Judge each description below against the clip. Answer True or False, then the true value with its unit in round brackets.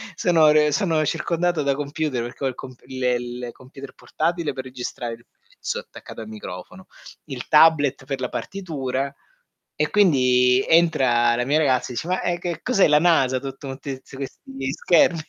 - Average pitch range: True (4.1 semitones)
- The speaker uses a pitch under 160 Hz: True (135 Hz)